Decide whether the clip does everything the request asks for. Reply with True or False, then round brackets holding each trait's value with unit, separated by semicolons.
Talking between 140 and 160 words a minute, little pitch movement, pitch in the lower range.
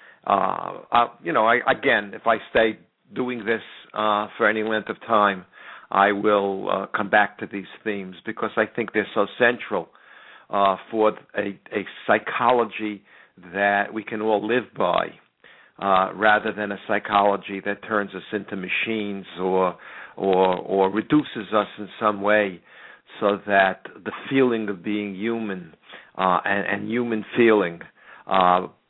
True (150 wpm; 1.9 semitones; 105 Hz)